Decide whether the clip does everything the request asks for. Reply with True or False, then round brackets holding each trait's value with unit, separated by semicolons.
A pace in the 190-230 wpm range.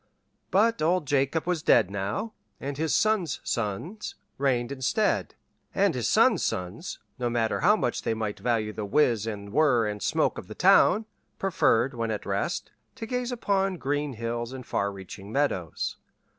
False (165 wpm)